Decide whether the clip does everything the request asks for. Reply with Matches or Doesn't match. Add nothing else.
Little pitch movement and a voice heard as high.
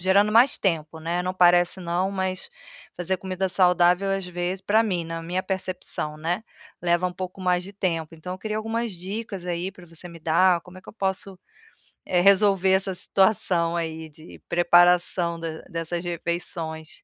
Doesn't match